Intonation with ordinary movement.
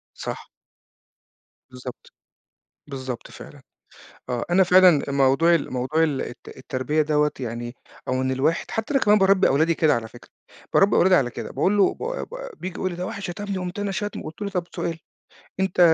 No: wide, 6.4 semitones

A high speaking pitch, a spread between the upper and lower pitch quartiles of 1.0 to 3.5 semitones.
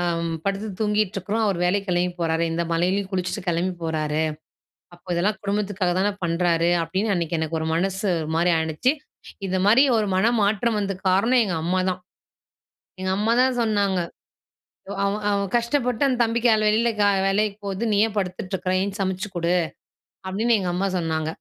Yes: high, 195 Hz; average, 3.2 semitones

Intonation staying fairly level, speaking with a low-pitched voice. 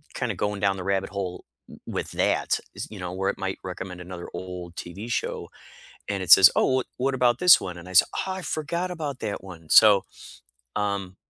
No: average, 4.4 semitones; very low, 95 Hz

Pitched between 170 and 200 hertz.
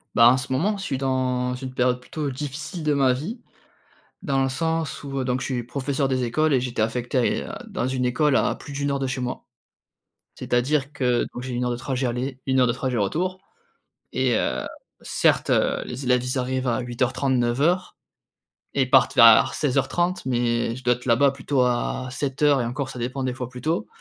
No: low, 130 Hz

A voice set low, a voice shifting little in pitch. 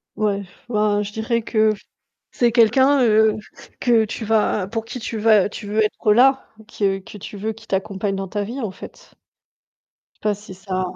No: high, 215 Hz; narrow, 1.9 semitones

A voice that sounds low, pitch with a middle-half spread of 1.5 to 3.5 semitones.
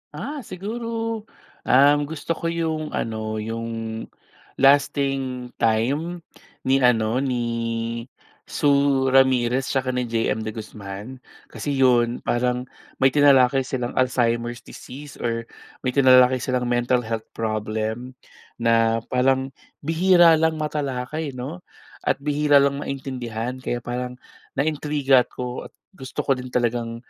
Yes: low, 130 Hz; average, 3.1 semitones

